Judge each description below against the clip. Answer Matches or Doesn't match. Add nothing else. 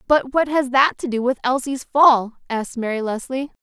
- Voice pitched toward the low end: Doesn't match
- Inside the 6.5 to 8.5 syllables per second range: Doesn't match